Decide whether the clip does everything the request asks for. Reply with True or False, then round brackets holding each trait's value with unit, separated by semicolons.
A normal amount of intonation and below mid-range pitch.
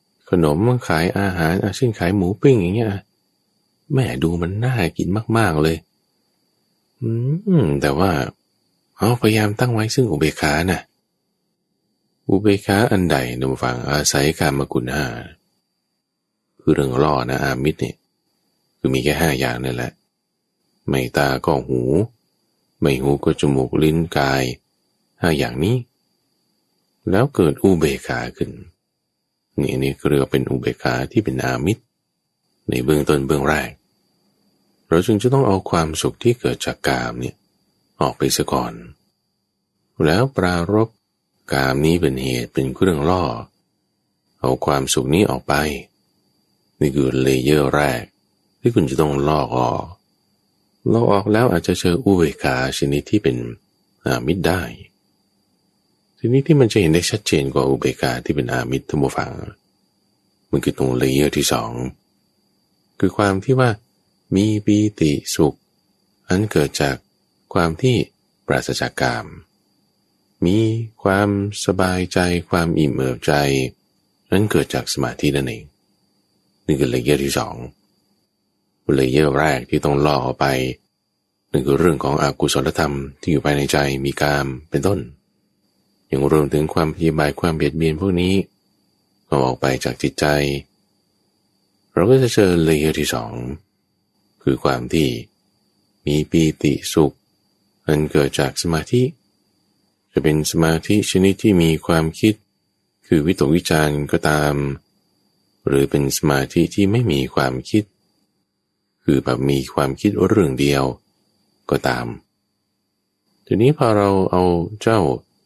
False (6.2 semitones; 80 Hz)